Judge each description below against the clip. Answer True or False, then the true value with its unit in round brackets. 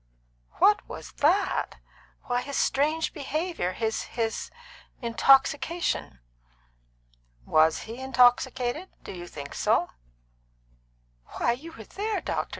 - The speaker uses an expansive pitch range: True (5.9 semitones)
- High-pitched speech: True (265 Hz)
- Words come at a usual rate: False (105 wpm)